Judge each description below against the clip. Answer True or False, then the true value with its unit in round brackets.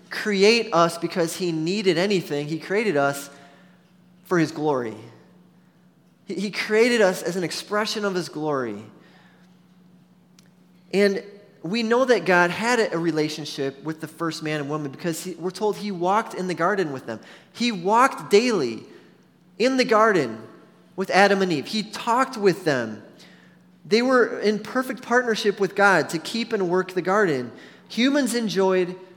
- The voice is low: False (185 Hz)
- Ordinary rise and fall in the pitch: True (3.6 semitones)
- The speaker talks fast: False (155 wpm)